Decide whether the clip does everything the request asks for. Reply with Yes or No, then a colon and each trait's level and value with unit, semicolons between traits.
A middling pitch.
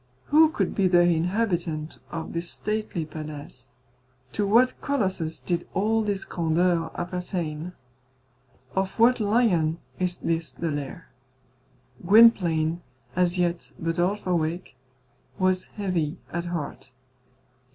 Yes: medium, 175 Hz